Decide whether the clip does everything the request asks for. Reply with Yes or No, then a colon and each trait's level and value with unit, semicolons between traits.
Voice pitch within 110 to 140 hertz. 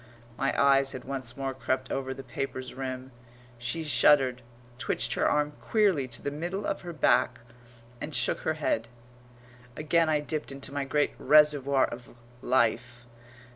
Yes: low, 135 Hz